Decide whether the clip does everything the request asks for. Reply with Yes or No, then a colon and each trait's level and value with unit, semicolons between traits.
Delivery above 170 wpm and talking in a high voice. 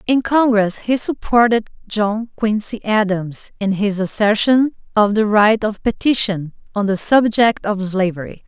No: average, 140 wpm; high, 215 Hz